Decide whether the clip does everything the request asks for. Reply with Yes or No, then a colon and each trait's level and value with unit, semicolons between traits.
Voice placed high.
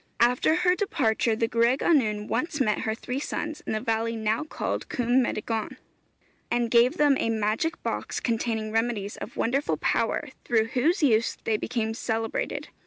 Yes: high, 230 Hz